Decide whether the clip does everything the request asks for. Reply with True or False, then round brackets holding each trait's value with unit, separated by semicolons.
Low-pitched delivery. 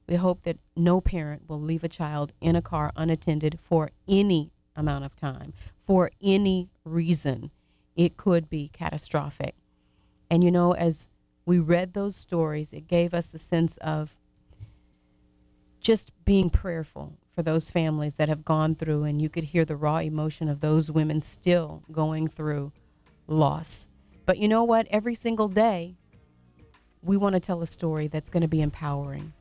False (160 Hz)